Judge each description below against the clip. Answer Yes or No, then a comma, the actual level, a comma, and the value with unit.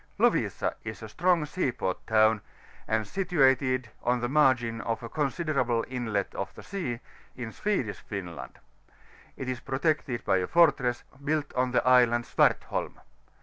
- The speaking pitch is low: Yes, low, 125 Hz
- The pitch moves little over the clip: No, average, 4.4 semitones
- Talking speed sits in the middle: Yes, average, 150 wpm